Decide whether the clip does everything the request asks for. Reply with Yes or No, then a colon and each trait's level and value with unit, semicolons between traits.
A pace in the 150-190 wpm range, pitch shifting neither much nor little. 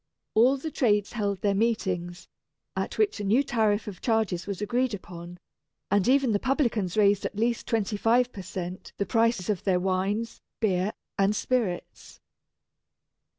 Yes: average, 155 wpm; average, 3.6 semitones